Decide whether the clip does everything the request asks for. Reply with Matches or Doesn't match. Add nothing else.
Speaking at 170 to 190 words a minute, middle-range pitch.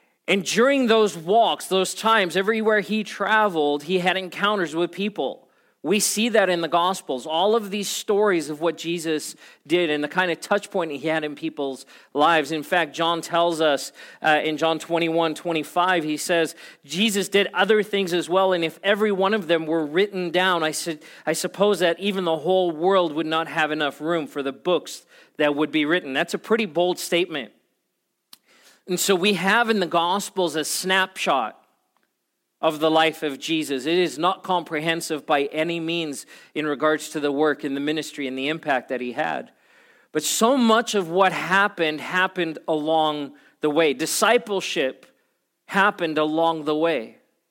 Matches